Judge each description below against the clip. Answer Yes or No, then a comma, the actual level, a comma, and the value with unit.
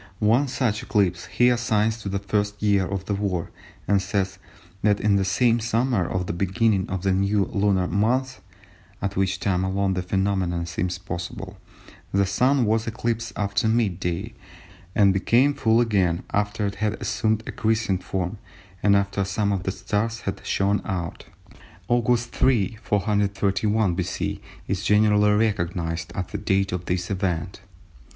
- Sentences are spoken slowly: No, average, 160 wpm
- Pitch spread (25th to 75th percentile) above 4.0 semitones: No, narrow, 2.6 semitones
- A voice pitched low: Yes, low, 100 Hz